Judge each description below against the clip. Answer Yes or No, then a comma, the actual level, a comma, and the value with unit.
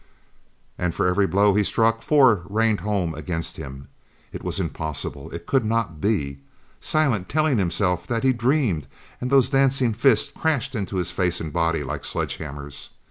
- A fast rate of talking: No, average, 165 wpm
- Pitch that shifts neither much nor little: No, wide, 6.7 semitones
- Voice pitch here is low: Yes, low, 100 Hz